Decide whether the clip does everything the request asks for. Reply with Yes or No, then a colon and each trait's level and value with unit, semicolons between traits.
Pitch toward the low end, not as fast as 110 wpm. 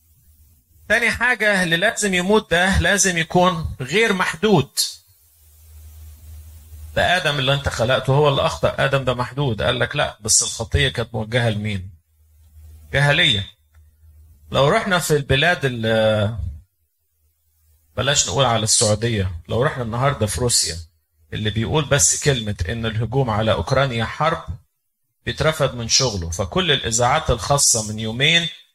No: low, 115 Hz; average, 125 wpm